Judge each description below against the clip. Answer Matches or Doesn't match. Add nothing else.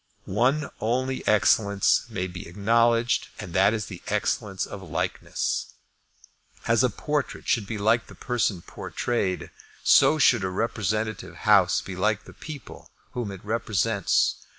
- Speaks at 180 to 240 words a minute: Doesn't match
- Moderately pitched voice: Doesn't match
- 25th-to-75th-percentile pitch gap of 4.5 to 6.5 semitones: Doesn't match